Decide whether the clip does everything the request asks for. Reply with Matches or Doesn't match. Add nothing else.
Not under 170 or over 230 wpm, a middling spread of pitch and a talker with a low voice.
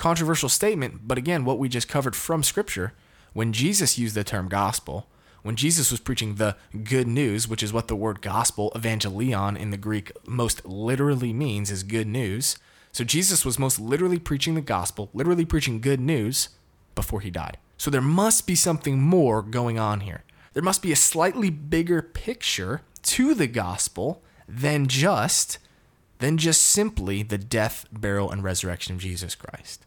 Doesn't match